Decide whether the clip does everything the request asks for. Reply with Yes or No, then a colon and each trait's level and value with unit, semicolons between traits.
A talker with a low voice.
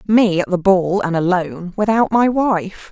No: high, 195 Hz